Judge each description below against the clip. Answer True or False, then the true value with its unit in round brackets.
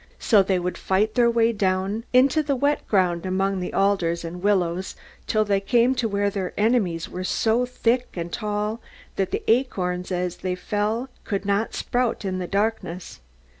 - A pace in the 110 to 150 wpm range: False (175 wpm)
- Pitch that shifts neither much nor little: True (3.7 semitones)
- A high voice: True (200 Hz)